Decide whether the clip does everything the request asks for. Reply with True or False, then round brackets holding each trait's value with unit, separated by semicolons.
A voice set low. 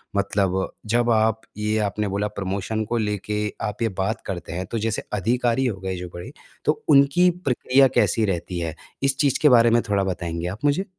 True (105 Hz)